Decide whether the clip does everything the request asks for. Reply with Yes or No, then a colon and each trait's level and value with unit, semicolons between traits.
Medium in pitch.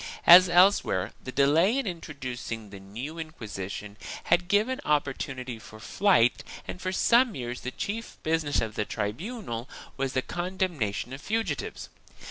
Yes: medium, 145 Hz